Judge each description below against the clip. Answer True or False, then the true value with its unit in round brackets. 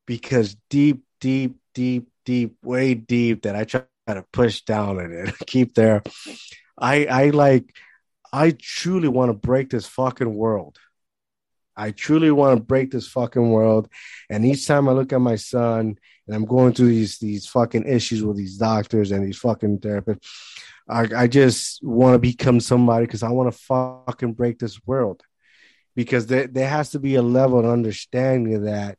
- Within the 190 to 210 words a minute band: False (180 wpm)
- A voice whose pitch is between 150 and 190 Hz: False (120 Hz)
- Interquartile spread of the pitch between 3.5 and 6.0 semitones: False (2.8 semitones)